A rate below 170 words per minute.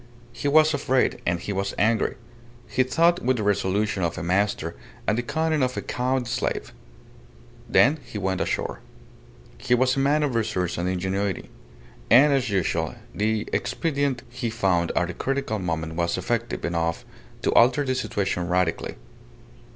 Yes: average, 160 wpm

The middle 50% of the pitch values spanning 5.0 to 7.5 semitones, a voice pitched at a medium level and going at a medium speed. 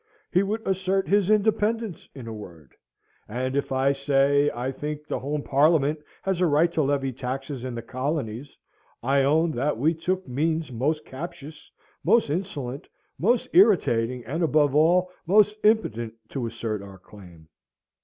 Yes: average, 5.3 semitones; medium, 145 Hz; average, 155 wpm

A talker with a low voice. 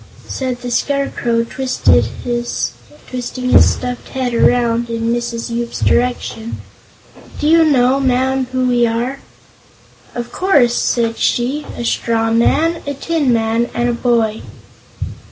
No: high, 245 Hz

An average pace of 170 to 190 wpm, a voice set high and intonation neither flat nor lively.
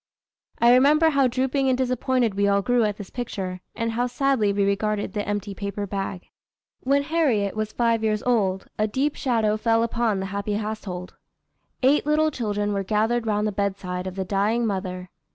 Yes: average, 185 wpm; high, 215 Hz; average, 3.7 semitones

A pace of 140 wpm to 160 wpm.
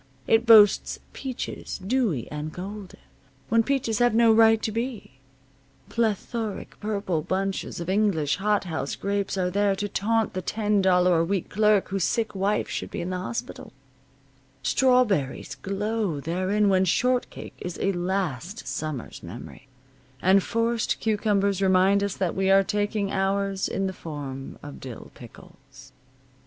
Yes: average, 145 wpm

